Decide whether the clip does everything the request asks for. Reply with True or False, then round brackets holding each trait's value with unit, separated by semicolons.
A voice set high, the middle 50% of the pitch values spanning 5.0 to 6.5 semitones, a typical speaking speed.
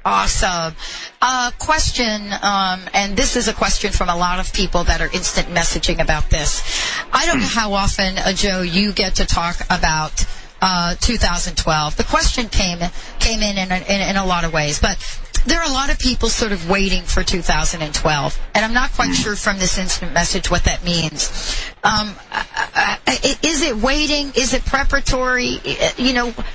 True (200 Hz; 5.4 semitones; 190 wpm)